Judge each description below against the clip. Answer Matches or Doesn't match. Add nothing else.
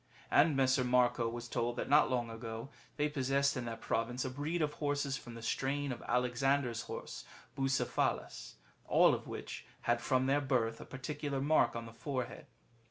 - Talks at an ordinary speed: Matches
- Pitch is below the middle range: Matches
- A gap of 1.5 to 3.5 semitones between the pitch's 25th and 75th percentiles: Matches